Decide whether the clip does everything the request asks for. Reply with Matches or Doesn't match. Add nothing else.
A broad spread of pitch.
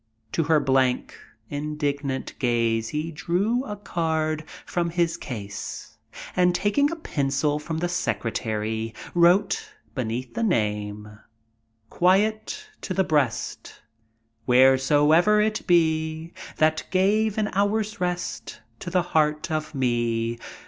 Matches